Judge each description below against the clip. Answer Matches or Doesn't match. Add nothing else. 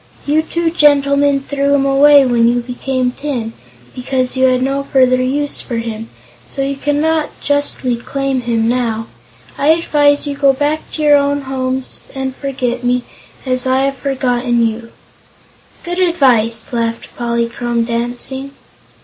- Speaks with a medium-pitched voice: Doesn't match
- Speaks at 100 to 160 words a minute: Matches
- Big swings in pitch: Doesn't match